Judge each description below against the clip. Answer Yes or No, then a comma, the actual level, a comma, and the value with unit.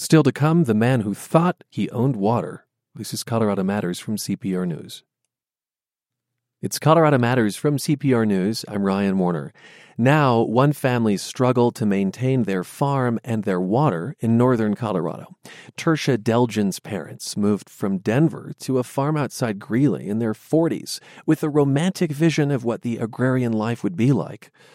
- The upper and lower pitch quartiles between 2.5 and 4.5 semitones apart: No, average, 4.9 semitones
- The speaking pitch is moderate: No, low, 120 Hz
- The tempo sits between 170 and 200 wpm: No, average, 160 wpm